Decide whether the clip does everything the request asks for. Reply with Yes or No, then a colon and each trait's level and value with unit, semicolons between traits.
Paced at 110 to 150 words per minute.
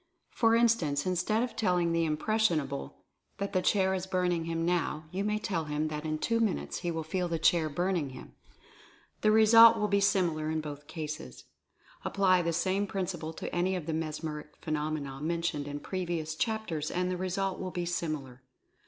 No: average, 185 wpm